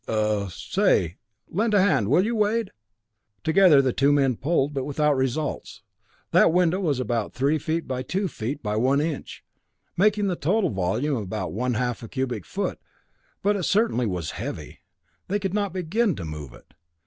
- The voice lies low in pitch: No, medium, 145 Hz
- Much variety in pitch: Yes, wide, 8.0 semitones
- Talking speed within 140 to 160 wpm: No, average, 175 wpm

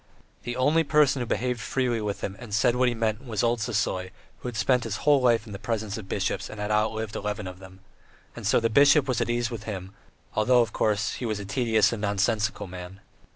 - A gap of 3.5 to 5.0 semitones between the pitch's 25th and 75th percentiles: No, average, 2.9 semitones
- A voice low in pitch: Yes, low, 110 Hz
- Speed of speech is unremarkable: No, fast, 235 wpm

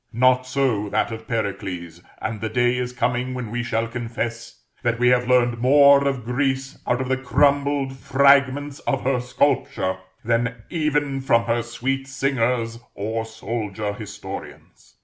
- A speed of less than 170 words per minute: Yes, average, 150 wpm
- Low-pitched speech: Yes, low, 125 Hz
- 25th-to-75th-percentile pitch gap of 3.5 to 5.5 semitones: No, average, 2.8 semitones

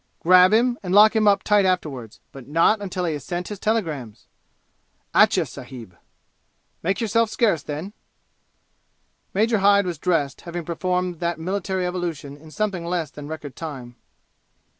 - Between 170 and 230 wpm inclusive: No, average, 150 wpm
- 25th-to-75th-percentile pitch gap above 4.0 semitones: Yes, average, 4.6 semitones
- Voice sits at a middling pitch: Yes, medium, 180 Hz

